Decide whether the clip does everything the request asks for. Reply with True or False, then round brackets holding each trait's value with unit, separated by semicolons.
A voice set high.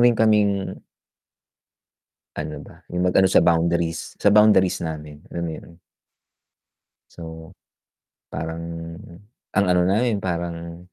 False (85 Hz)